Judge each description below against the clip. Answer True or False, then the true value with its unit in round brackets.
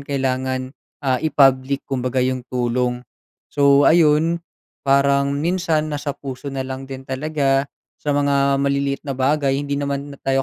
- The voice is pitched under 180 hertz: True (140 Hz)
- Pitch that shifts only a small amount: True (1.4 semitones)